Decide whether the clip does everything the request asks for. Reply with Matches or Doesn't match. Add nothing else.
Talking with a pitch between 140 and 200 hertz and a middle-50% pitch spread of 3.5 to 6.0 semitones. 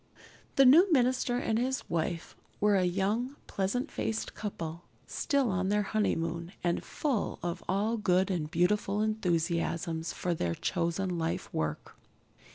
Matches